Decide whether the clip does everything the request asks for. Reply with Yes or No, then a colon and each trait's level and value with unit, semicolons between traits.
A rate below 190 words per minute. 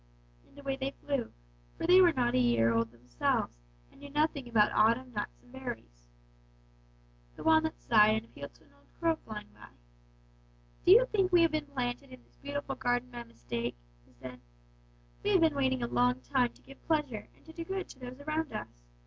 No: average, 200 wpm